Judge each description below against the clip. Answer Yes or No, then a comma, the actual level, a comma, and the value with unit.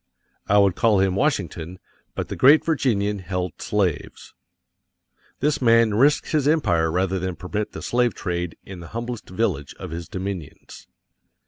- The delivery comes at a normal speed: Yes, average, 150 wpm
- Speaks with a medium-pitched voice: No, low, 100 Hz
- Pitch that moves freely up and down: No, average, 4.7 semitones